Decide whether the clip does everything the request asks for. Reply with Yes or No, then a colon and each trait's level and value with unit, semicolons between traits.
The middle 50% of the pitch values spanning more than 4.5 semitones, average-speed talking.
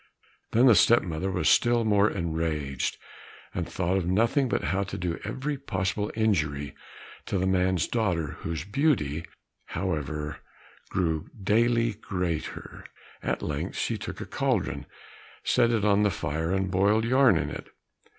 Yes: average, 5.2 semitones; average, 150 wpm